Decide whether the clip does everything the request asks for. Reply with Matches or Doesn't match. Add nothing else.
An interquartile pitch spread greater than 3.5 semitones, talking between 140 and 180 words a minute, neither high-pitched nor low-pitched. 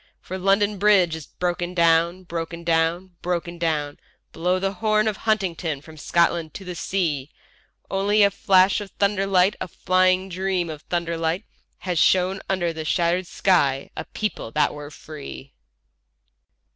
Doesn't match